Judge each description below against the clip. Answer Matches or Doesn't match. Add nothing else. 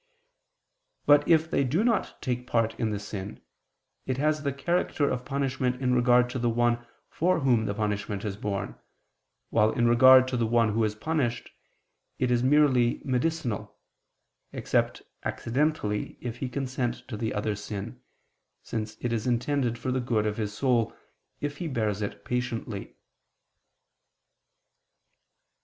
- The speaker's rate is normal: Matches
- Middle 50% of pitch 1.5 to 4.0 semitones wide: Matches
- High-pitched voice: Doesn't match